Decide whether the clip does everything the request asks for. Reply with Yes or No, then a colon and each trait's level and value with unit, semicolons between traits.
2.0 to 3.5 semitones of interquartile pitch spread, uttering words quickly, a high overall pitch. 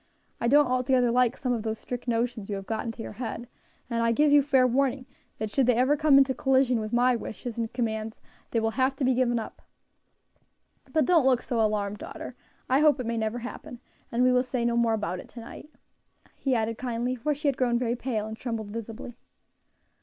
Yes: narrow, 2.4 semitones; fast, 220 wpm; high, 240 Hz